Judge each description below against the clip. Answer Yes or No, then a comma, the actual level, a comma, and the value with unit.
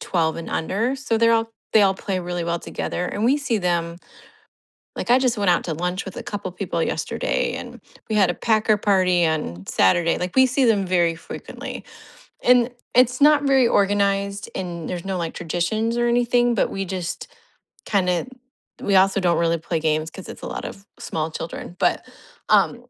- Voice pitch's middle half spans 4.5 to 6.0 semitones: Yes, average, 5.1 semitones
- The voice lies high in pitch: Yes, high, 195 Hz